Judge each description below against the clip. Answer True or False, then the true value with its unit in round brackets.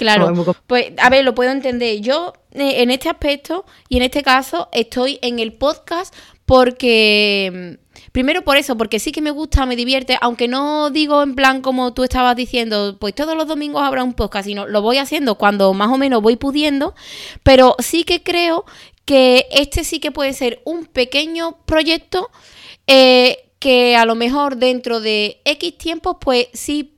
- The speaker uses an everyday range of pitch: True (3.8 semitones)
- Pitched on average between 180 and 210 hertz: False (260 Hz)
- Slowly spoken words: False (180 wpm)